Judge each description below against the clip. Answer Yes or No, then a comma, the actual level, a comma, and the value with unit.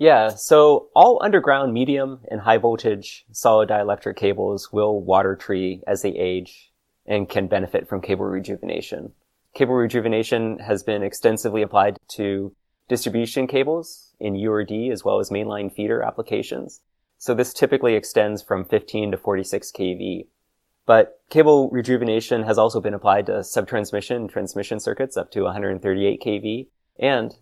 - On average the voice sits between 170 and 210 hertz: No, low, 110 Hz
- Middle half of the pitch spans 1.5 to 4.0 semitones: Yes, average, 3.6 semitones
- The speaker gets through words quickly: No, average, 145 wpm